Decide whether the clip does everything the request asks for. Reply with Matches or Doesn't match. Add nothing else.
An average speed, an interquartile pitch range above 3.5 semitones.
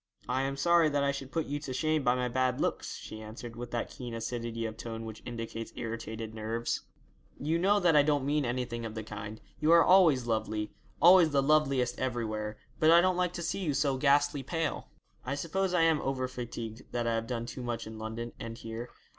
Doesn't match